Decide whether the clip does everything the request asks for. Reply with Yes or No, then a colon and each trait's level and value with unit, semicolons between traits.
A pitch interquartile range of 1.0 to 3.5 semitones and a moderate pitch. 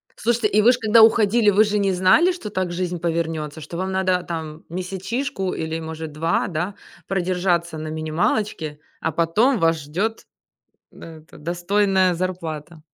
No: average, 4.0 semitones; medium, 180 Hz